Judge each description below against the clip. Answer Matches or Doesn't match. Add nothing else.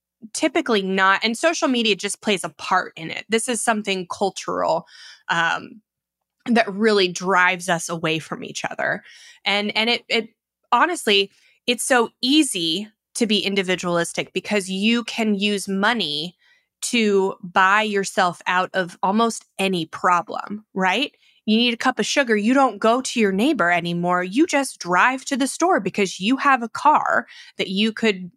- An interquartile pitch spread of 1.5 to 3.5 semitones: Doesn't match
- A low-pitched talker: Doesn't match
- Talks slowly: Doesn't match